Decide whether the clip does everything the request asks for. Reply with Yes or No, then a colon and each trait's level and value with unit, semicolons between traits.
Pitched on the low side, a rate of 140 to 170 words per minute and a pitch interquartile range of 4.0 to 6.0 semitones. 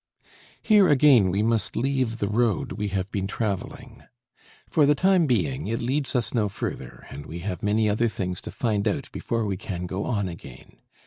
No: low, 110 Hz; average, 190 wpm; average, 4.3 semitones